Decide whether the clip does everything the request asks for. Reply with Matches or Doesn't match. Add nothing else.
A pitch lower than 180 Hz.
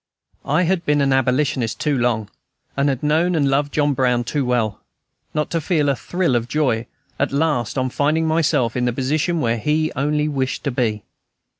Matches